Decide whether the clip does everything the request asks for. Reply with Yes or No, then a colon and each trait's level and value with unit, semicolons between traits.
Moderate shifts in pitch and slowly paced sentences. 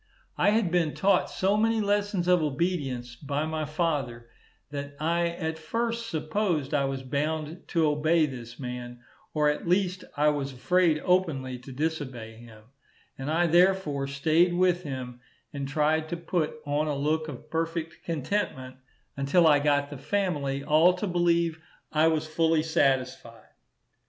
No: average, 3.8 semitones; average, 155 wpm